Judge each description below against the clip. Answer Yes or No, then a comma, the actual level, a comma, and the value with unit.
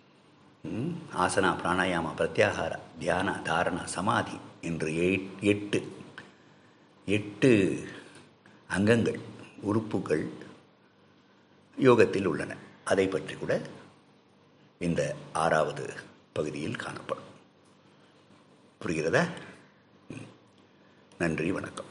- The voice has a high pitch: No, very low, 95 Hz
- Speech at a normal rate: No, slow, 65 wpm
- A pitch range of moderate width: Yes, average, 3.4 semitones